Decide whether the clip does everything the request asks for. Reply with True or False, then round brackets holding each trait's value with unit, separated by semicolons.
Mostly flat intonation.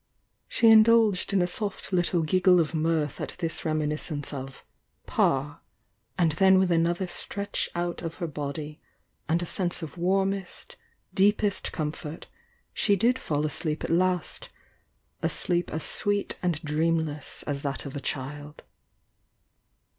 False (3.8 semitones)